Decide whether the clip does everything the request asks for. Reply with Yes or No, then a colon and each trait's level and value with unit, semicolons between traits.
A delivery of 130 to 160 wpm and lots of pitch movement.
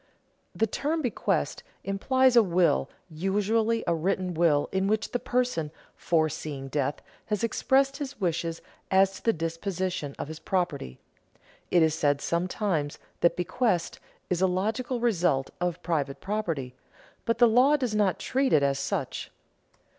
Yes: average, 150 wpm; wide, 5.9 semitones